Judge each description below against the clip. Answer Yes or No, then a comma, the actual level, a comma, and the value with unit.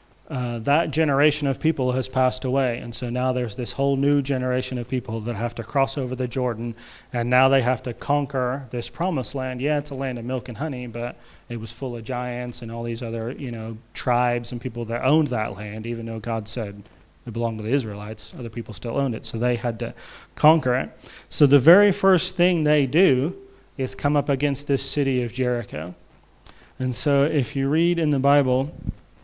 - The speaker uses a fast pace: Yes, fast, 220 wpm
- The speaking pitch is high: No, low, 125 Hz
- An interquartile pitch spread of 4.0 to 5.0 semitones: No, average, 2.8 semitones